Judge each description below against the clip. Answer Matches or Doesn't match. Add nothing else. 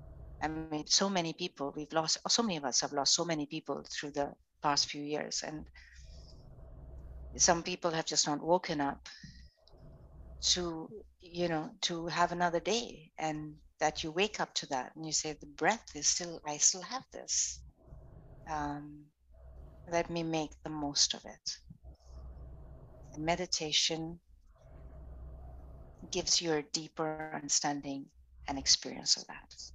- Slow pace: Doesn't match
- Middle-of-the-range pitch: Matches